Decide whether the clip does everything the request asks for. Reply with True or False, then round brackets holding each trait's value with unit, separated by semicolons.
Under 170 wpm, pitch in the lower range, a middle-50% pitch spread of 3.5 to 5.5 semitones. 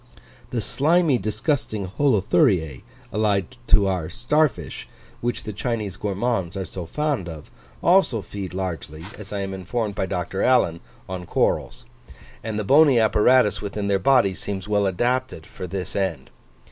True (150 wpm; 105 Hz; 4.5 semitones)